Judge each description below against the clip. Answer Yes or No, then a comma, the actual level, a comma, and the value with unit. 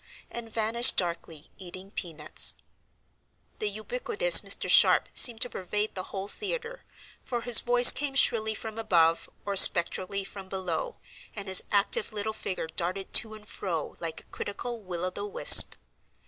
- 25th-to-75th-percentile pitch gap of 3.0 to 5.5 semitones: Yes, average, 4.3 semitones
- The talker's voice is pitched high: Yes, high, 205 Hz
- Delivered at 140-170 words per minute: Yes, average, 160 wpm